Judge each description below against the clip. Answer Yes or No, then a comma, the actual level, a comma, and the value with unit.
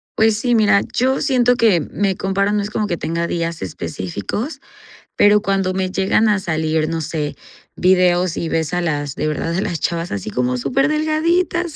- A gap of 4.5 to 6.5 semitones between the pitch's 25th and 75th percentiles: Yes, average, 5.2 semitones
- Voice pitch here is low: No, medium, 185 Hz